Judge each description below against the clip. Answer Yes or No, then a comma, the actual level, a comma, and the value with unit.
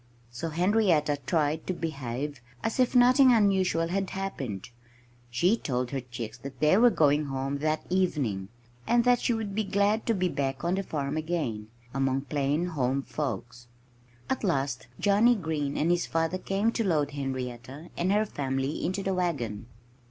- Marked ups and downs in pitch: Yes, wide, 6.3 semitones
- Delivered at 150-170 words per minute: Yes, average, 165 wpm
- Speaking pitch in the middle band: Yes, medium, 155 Hz